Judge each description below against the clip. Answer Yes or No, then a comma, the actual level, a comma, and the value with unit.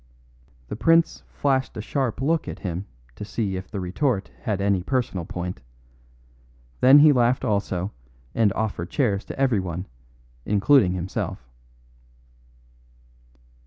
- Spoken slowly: Yes, slow, 125 wpm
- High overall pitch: No, low, 105 Hz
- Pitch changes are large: Yes, wide, 6.0 semitones